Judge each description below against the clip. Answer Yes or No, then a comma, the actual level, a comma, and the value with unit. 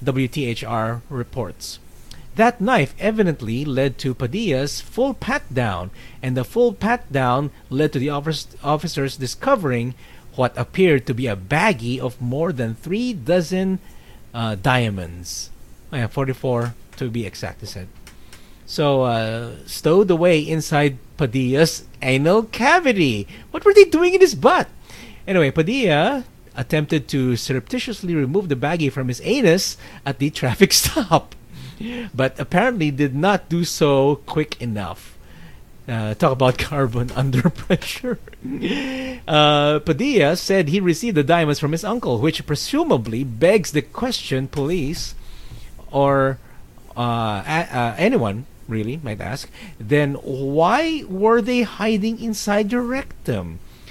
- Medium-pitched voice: Yes, medium, 145 Hz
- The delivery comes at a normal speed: No, slow, 130 wpm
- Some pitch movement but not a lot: No, wide, 7.0 semitones